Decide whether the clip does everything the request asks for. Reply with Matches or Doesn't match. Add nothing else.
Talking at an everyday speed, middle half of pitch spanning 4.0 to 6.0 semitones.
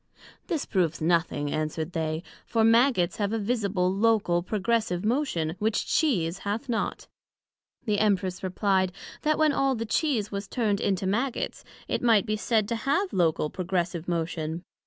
Matches